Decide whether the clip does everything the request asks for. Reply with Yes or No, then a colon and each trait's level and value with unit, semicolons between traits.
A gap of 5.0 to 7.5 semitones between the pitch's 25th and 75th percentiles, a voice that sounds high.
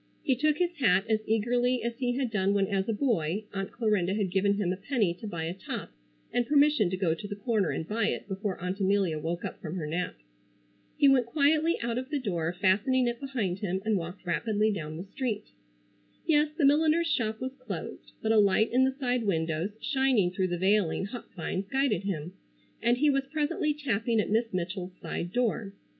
Yes: average, 5.3 semitones; high, 215 Hz